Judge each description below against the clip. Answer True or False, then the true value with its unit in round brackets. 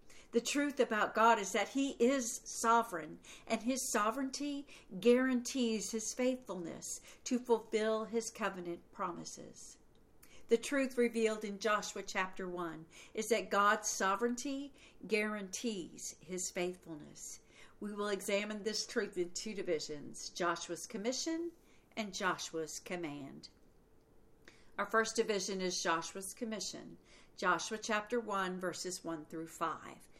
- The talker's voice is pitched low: False (215 Hz)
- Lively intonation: False (4.3 semitones)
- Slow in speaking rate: True (120 wpm)